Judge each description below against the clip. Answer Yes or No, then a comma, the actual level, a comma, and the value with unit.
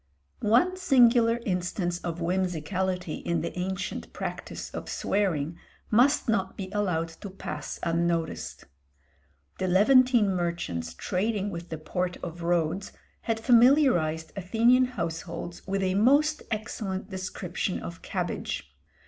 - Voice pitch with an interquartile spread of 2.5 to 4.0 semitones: No, average, 4.6 semitones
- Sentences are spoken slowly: Yes, slow, 120 wpm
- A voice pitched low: No, medium, 185 Hz